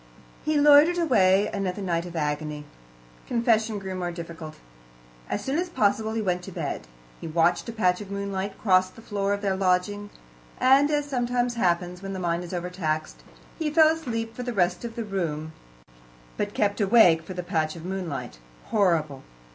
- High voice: Yes, high, 195 Hz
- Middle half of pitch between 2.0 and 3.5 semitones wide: No, average, 4.6 semitones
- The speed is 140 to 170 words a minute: No, average, 180 wpm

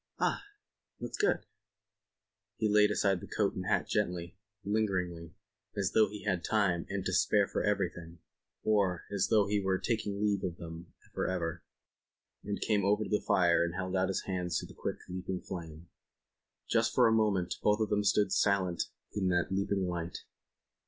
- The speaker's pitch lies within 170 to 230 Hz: No, very low, 95 Hz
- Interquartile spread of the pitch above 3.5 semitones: No, average, 2.7 semitones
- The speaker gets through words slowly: No, average, 180 wpm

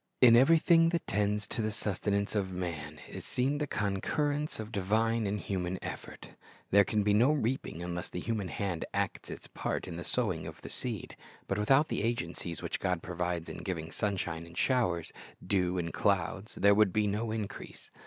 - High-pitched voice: No, low, 100 Hz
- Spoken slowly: No, average, 185 wpm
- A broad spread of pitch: No, average, 4.2 semitones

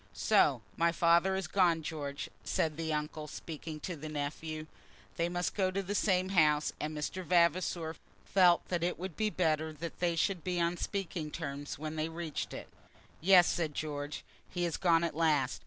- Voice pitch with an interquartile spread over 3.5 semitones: No, narrow, 2.5 semitones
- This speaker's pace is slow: No, average, 185 wpm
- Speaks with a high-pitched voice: No, medium, 165 Hz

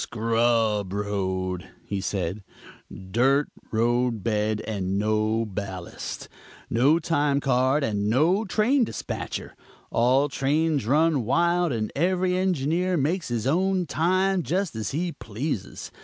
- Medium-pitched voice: No, low, 130 Hz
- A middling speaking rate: No, slow, 120 wpm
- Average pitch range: No, wide, 7.6 semitones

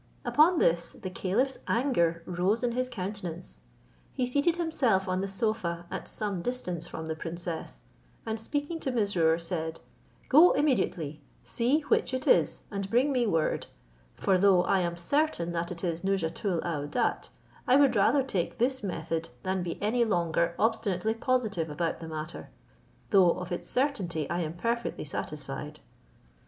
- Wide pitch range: Yes, wide, 6.5 semitones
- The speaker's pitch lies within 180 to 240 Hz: Yes, high, 190 Hz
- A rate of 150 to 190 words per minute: Yes, average, 155 wpm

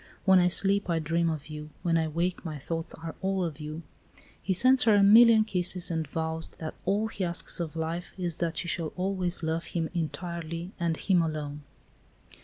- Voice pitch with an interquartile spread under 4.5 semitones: Yes, narrow, 2.6 semitones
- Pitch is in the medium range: Yes, medium, 170 Hz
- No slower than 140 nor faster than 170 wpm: No, average, 200 wpm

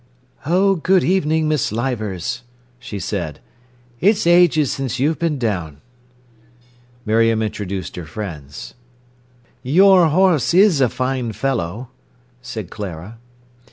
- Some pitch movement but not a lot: No, wide, 7.7 semitones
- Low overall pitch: Yes, low, 125 Hz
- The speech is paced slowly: Yes, slow, 110 wpm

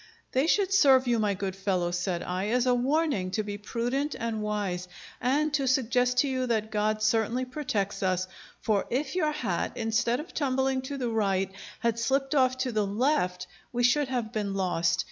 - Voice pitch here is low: No, high, 235 Hz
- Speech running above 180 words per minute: Yes, average, 190 wpm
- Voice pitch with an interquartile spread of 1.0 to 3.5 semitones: No, average, 4.5 semitones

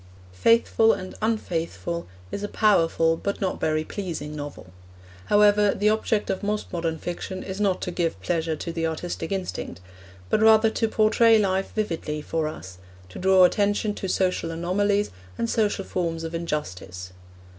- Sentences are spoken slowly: No, average, 155 wpm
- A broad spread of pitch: No, average, 4.1 semitones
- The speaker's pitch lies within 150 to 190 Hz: Yes, medium, 185 Hz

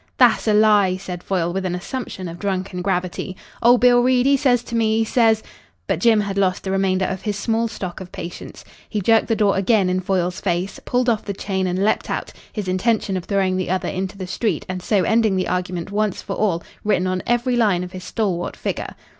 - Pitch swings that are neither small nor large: Yes, average, 3.2 semitones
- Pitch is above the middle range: Yes, high, 195 Hz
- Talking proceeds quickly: Yes, fast, 230 wpm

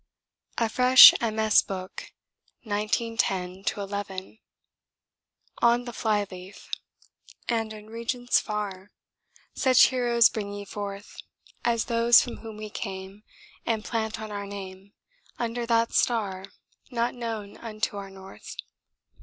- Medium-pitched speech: No, high, 215 Hz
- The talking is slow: Yes, slow, 110 wpm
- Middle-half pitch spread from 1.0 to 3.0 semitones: Yes, average, 2.7 semitones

